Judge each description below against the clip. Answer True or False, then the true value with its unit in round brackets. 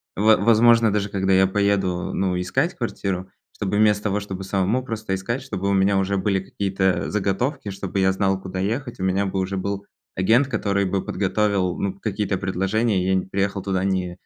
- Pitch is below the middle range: True (100 Hz)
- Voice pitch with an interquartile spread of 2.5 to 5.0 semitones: False (1.8 semitones)